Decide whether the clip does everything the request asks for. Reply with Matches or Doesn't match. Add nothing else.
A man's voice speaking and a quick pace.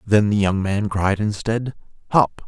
Doesn't match